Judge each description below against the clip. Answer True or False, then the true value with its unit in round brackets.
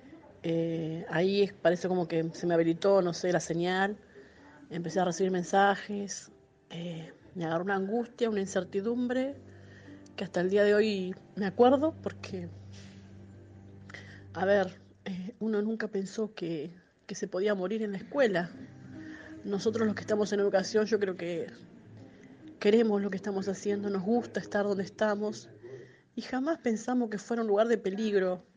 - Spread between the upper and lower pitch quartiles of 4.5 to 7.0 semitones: False (4.1 semitones)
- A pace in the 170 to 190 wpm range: False (155 wpm)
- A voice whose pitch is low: False (195 Hz)